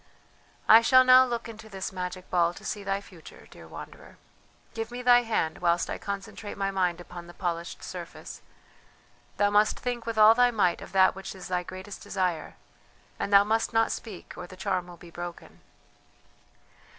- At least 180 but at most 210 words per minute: Yes, average, 185 wpm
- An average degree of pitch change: Yes, average, 3.9 semitones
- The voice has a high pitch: Yes, high, 195 Hz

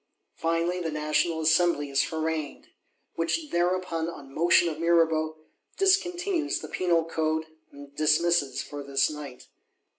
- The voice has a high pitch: No, medium, 165 Hz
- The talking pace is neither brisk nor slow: No, slow, 125 wpm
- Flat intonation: Yes, narrow, 2.2 semitones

